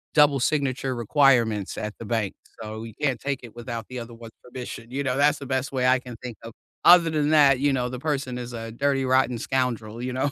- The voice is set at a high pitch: No, low, 125 Hz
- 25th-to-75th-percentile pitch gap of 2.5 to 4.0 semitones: Yes, average, 2.9 semitones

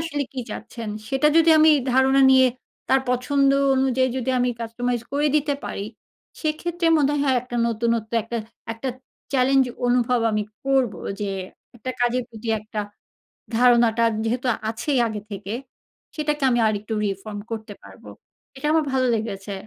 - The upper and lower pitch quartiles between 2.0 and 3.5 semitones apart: Yes, average, 3.2 semitones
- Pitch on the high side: Yes, very high, 250 Hz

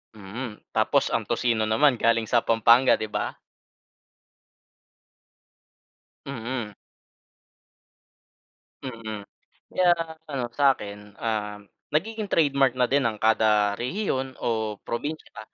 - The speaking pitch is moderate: No, low, 115 Hz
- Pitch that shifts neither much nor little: Yes, average, 3.7 semitones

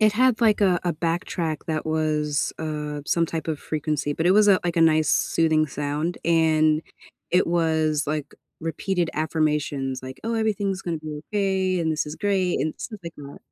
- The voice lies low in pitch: No, medium, 160 Hz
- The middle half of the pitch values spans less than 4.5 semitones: Yes, average, 3.1 semitones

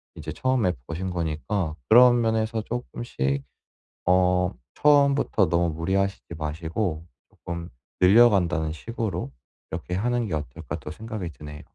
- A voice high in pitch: No, very low, 90 Hz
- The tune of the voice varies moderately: No, wide, 5.7 semitones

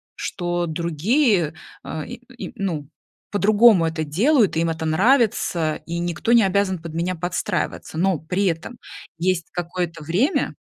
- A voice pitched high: No, medium, 175 Hz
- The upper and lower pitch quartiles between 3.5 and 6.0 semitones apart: Yes, average, 3.8 semitones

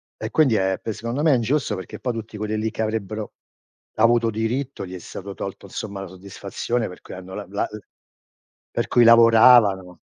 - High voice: No, low, 110 Hz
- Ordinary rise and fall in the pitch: Yes, average, 3.1 semitones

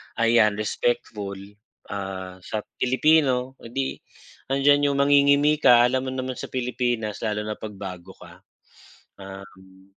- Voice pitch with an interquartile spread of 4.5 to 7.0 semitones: Yes, average, 4.9 semitones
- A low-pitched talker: Yes, low, 120 Hz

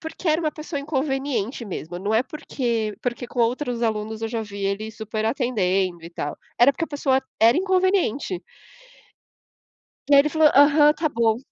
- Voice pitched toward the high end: Yes, high, 240 Hz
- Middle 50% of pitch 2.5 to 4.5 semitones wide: No, average, 5.3 semitones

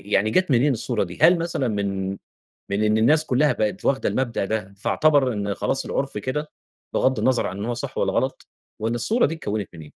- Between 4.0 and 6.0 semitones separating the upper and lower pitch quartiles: Yes, average, 5.2 semitones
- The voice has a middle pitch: No, low, 115 Hz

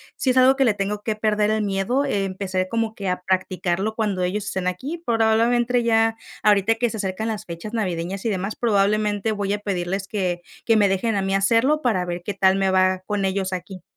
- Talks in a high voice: Yes, high, 205 Hz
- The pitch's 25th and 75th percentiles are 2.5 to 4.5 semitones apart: Yes, average, 2.9 semitones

